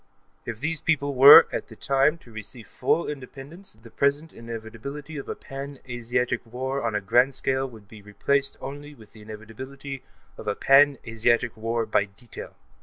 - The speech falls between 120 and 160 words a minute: No, average, 175 wpm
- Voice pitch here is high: No, low, 125 Hz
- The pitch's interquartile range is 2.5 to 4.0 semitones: Yes, average, 3.7 semitones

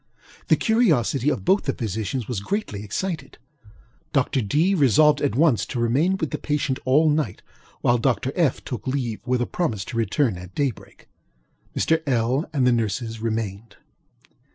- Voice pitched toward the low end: Yes, low, 130 Hz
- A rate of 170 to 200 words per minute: No, average, 160 wpm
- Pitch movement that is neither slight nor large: Yes, average, 4.9 semitones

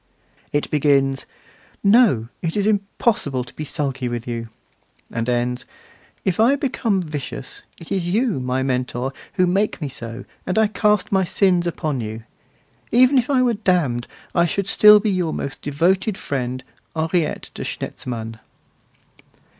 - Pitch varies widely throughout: Yes, wide, 7.7 semitones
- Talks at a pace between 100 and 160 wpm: Yes, average, 150 wpm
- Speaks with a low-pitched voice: No, medium, 165 Hz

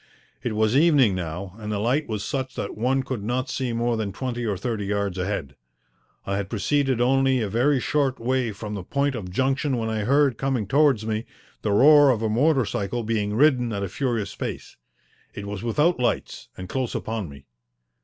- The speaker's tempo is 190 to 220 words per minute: Yes, average, 200 wpm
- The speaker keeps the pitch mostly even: No, average, 4.3 semitones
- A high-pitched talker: No, low, 115 Hz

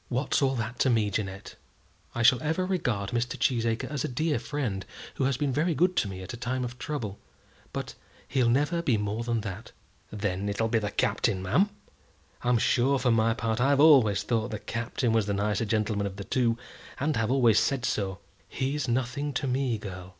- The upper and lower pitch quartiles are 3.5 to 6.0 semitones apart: Yes, average, 4.1 semitones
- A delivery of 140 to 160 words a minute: No, average, 200 wpm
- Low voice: Yes, low, 120 Hz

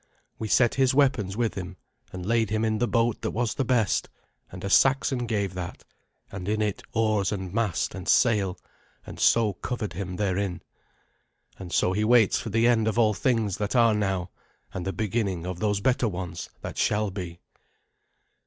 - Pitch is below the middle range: Yes, low, 105 Hz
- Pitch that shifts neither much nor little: Yes, average, 3.4 semitones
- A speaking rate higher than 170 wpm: Yes, average, 185 wpm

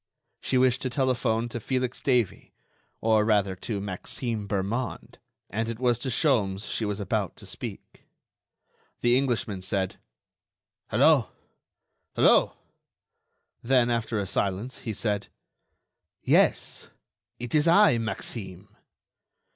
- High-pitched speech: No, low, 115 Hz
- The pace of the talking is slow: Yes, slow, 115 wpm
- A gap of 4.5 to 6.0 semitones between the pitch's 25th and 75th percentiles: No, average, 3.6 semitones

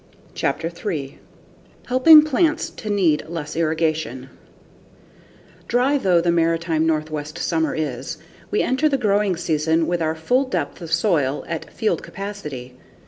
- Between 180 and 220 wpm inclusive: No, slow, 135 wpm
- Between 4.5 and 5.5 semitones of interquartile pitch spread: Yes, average, 4.9 semitones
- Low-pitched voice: No, medium, 165 Hz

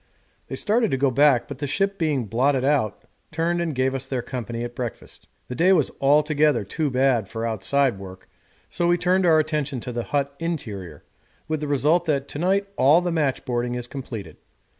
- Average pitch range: Yes, average, 4.4 semitones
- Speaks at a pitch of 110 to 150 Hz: Yes, medium, 140 Hz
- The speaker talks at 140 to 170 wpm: No, average, 195 wpm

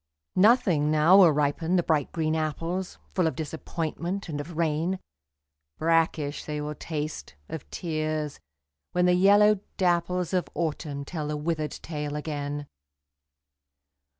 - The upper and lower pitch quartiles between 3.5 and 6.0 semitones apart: No, average, 2.8 semitones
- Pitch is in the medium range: Yes, medium, 160 Hz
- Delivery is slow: Yes, slow, 130 wpm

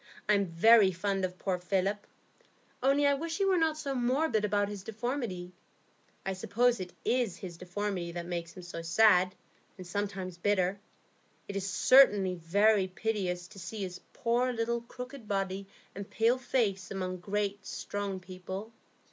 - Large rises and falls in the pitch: No, average, 3.9 semitones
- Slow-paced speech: No, average, 155 wpm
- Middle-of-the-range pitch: No, high, 200 Hz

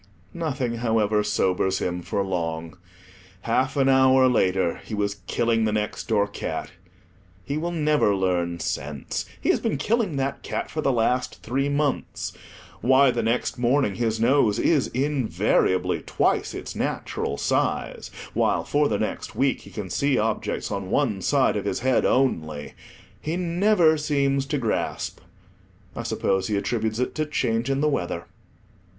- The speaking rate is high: No, average, 155 wpm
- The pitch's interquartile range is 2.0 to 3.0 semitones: No, wide, 5.5 semitones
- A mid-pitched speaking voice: No, low, 120 Hz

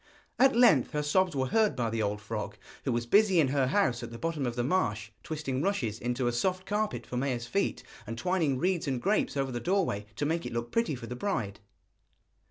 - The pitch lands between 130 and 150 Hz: Yes, low, 135 Hz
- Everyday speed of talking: No, fast, 225 wpm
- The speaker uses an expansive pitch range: Yes, wide, 7.7 semitones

